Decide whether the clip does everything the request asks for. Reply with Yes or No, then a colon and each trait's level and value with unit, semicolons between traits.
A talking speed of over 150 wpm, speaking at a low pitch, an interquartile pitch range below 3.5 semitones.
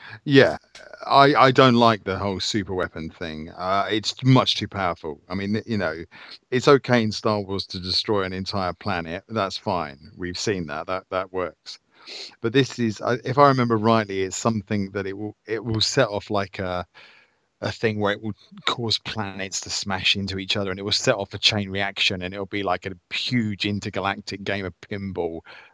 Yes: average, 200 wpm; low, 100 Hz; average, 2.7 semitones